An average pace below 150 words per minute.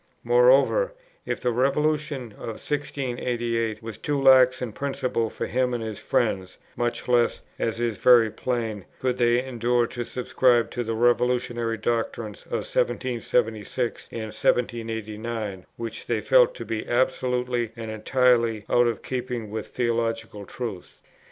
Yes: average, 140 wpm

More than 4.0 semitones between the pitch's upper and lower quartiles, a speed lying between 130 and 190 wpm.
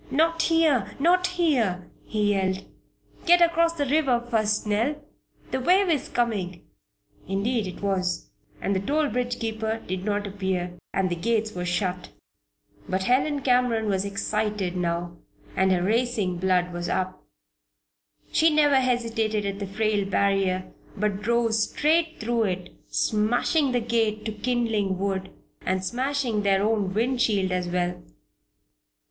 Yes: average, 4.7 semitones; average, 145 wpm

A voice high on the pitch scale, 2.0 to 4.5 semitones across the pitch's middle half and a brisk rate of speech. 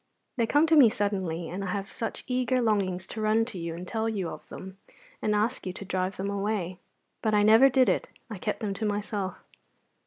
Yes: high, 205 Hz; average, 3.0 semitones; fast, 220 wpm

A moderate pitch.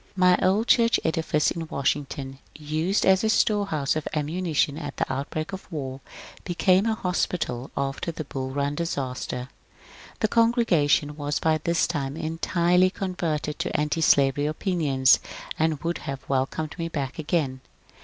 Yes: medium, 155 Hz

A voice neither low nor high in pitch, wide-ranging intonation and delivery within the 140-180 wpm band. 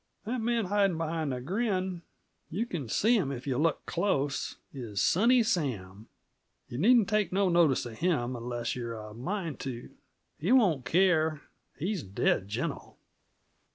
Yes: medium, 160 Hz; wide, 8.1 semitones; average, 155 wpm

